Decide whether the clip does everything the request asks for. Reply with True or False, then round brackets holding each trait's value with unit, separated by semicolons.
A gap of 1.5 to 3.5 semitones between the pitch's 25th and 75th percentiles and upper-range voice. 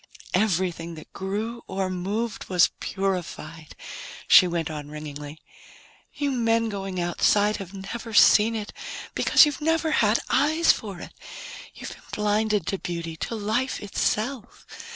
False (4.5 semitones; 200 Hz)